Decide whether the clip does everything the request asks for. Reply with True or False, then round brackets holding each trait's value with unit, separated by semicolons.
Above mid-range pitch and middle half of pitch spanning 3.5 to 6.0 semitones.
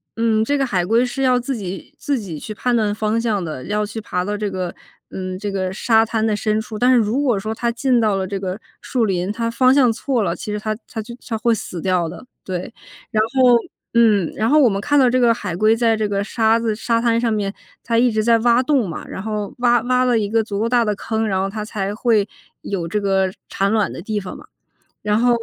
False (220 Hz; 2.9 semitones)